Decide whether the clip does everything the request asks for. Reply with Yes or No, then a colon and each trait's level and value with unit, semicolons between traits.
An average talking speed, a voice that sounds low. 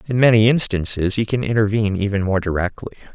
Yes: average, 170 wpm; low, 105 Hz